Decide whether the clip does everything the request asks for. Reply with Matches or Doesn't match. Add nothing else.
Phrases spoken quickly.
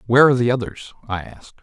Matches